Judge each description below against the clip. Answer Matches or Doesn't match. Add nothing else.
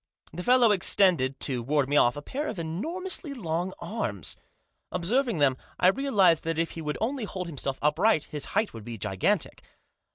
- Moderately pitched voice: Matches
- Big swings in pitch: Matches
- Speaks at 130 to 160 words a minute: Doesn't match